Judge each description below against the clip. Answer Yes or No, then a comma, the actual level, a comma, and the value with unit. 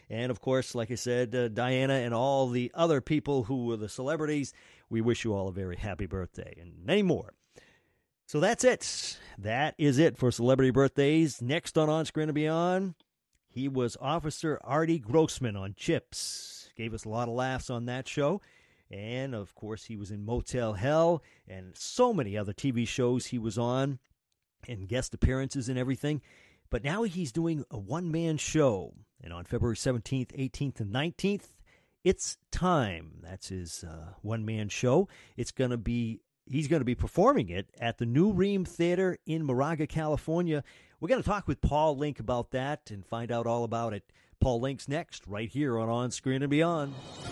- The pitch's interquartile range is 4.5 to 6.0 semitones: Yes, average, 5.1 semitones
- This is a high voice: No, low, 130 Hz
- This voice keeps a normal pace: Yes, average, 185 wpm